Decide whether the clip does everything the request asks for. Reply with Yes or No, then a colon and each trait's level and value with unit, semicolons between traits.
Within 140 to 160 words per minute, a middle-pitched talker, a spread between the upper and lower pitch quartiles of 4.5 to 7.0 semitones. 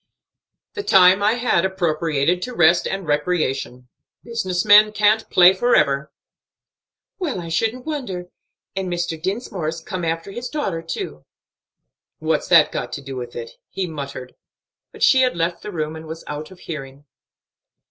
Yes: average, 155 wpm; medium, 175 Hz; average, 4.9 semitones